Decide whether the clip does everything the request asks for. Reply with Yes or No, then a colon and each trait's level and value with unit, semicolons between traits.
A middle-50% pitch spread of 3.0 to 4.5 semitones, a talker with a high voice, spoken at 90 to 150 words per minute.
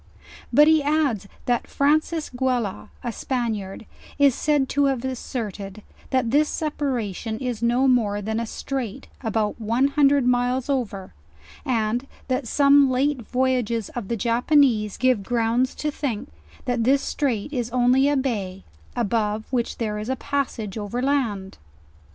Yes: average, 3.8 semitones; high, 245 Hz; average, 145 wpm